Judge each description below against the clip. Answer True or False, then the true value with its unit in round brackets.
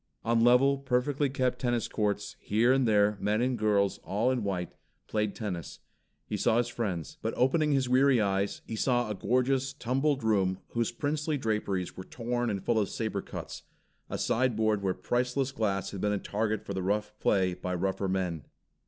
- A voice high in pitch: False (110 Hz)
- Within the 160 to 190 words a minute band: True (185 wpm)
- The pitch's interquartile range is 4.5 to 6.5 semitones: False (4.1 semitones)